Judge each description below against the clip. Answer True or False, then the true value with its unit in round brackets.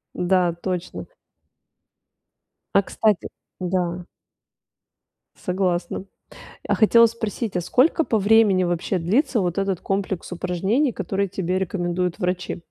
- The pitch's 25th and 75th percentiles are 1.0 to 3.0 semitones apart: True (2.6 semitones)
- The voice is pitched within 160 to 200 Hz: True (185 Hz)